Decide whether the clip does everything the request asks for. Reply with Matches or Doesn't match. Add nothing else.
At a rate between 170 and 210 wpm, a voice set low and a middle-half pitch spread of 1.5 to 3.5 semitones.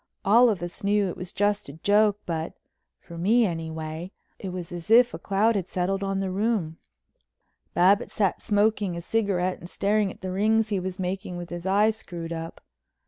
Doesn't match